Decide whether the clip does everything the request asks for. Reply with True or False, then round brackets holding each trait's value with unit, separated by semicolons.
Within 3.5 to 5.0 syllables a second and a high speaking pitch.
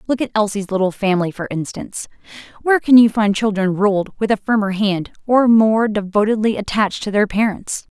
False (5.6 syllables/s; 210 Hz)